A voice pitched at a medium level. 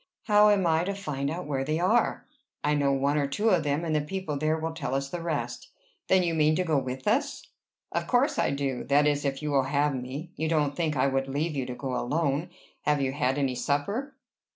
Yes: medium, 150 Hz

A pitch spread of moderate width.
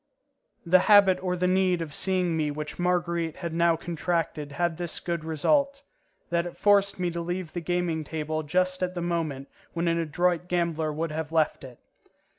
No: narrow, 2.1 semitones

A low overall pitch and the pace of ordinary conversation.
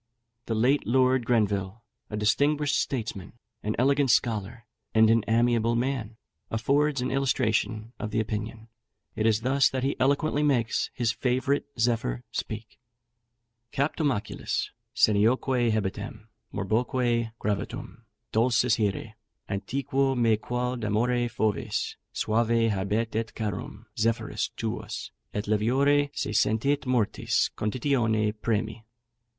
No: low, 115 Hz; slow, 115 wpm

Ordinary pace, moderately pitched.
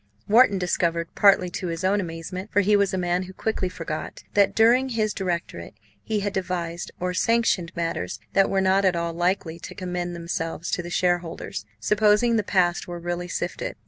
Yes: average, 185 wpm; medium, 180 Hz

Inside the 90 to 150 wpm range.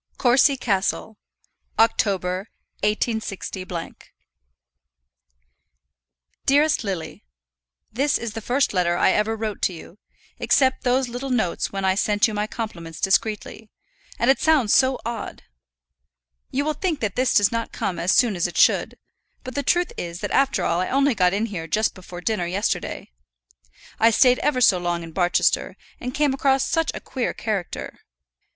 No: average, 160 wpm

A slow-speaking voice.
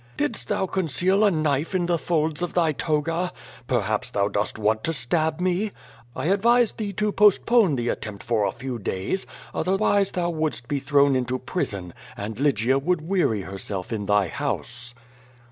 No: average, 170 wpm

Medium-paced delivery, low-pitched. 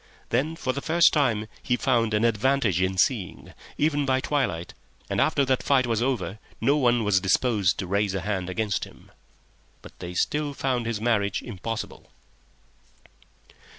Yes: average, 160 wpm; low, 115 Hz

